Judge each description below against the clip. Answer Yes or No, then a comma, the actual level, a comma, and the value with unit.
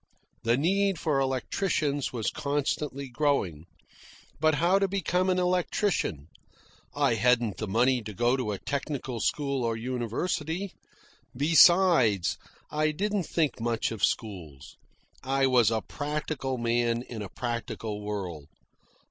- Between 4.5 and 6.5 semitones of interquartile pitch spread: Yes, average, 5.2 semitones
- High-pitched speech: No, low, 130 Hz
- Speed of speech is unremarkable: No, slow, 130 wpm